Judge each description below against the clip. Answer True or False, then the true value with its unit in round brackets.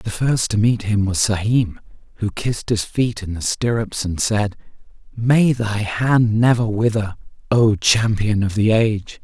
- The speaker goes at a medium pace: True (170 wpm)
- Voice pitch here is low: True (110 Hz)